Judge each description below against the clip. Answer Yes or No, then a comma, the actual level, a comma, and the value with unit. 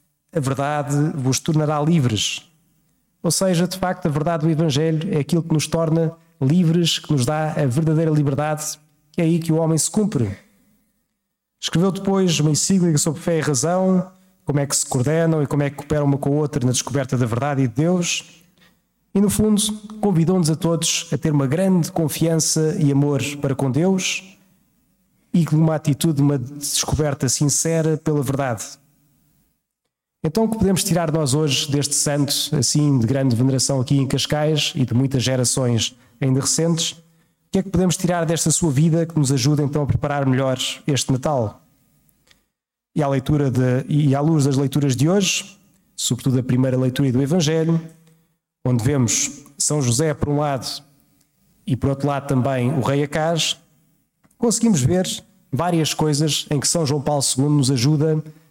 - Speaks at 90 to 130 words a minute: No, average, 175 wpm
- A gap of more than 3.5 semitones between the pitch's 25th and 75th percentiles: No, average, 3.1 semitones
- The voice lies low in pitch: No, medium, 155 Hz